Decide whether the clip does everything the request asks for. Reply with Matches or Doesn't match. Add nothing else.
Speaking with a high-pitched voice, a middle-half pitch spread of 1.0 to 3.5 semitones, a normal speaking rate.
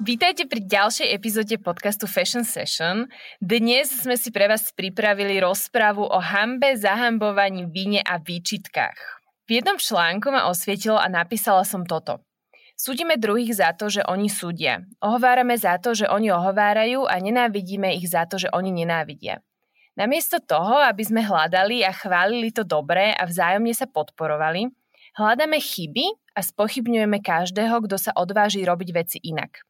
Doesn't match